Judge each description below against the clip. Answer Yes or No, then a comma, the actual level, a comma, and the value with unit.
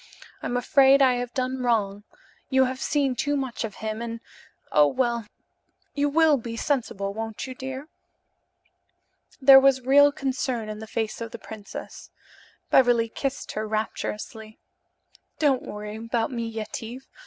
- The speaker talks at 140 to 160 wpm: Yes, average, 145 wpm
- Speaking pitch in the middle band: No, high, 245 Hz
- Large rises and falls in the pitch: No, average, 3.3 semitones